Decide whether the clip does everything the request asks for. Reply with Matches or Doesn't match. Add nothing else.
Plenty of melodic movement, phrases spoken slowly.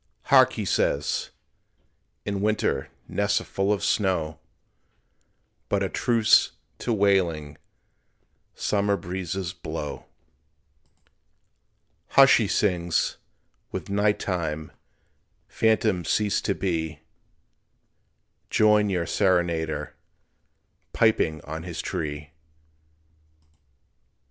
Doesn't match